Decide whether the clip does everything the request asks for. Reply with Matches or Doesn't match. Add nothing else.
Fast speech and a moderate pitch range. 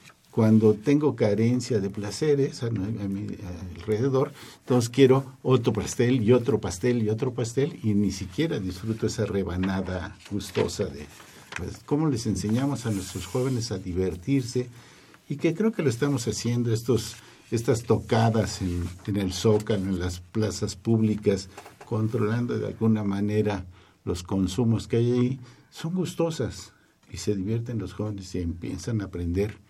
Doesn't match